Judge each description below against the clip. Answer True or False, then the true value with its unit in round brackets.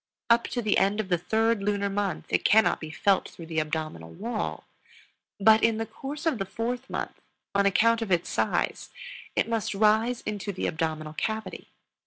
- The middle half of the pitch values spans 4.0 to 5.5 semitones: False (3.4 semitones)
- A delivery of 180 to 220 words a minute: True (185 wpm)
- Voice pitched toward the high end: True (210 Hz)